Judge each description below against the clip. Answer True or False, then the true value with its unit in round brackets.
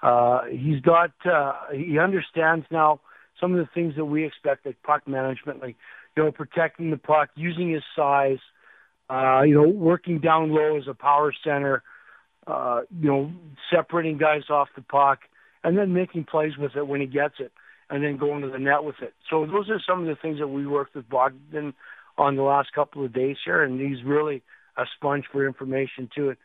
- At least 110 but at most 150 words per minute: False (205 wpm)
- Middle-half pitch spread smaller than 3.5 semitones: True (2.4 semitones)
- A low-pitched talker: False (145 Hz)